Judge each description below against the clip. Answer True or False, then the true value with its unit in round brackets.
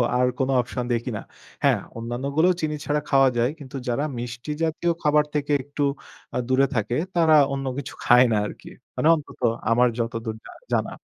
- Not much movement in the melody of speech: False (3.7 semitones)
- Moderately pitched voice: False (130 Hz)